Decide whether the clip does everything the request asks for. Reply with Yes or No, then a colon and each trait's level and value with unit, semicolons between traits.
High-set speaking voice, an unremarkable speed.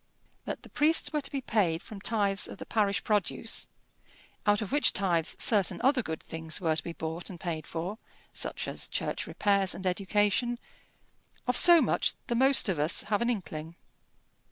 Yes: high, 200 Hz; average, 180 wpm